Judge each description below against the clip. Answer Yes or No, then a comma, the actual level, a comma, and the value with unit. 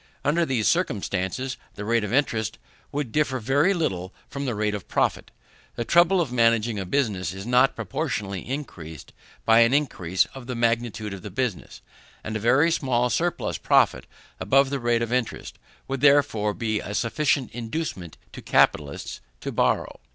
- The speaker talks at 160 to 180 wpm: Yes, average, 165 wpm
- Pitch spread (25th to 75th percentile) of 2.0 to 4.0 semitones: No, average, 4.8 semitones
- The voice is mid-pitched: No, low, 120 Hz